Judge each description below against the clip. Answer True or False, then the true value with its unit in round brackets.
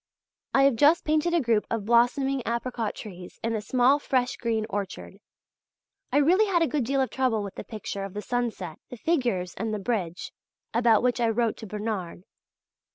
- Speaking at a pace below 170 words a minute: False (190 wpm)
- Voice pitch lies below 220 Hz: False (235 Hz)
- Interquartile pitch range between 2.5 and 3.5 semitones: False (4.1 semitones)